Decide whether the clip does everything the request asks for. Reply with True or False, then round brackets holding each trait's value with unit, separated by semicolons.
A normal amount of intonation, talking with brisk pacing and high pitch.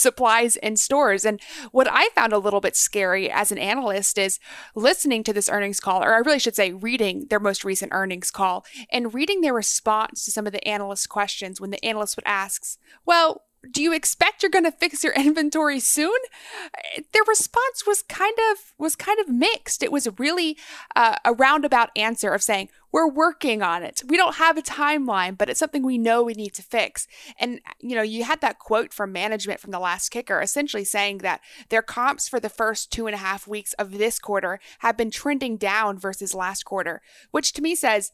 False (6.6 semitones; 210 wpm; 230 Hz)